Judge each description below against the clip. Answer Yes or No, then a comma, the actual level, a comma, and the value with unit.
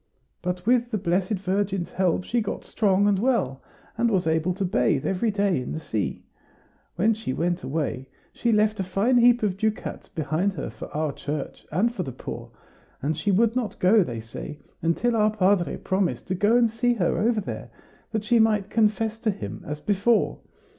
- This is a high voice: Yes, high, 195 Hz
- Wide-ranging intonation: No, average, 4.4 semitones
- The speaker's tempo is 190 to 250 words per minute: Yes, average, 195 wpm